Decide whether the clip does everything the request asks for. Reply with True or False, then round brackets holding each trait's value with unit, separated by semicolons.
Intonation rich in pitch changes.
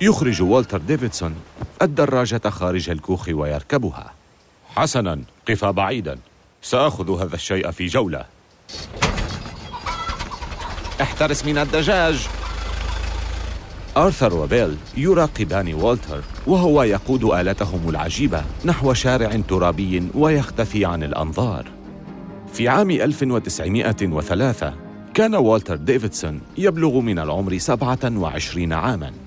True (7.1 semitones)